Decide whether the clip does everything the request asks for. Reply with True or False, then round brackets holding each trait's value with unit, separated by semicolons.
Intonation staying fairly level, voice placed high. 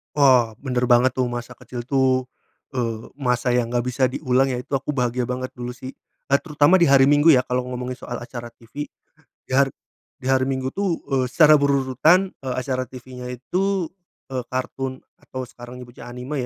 False (1.8 semitones; 130 Hz)